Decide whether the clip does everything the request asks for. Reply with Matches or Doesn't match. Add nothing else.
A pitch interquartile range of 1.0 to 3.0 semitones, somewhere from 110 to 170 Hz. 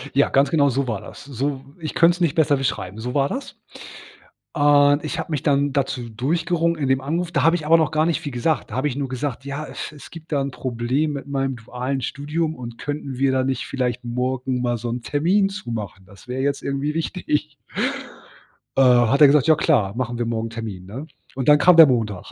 Doesn't match